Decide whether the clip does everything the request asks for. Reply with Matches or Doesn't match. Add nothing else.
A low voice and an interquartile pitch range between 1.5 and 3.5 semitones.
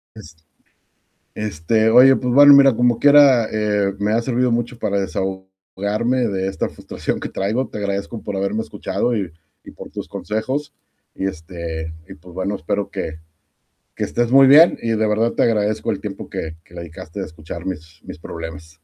Doesn't match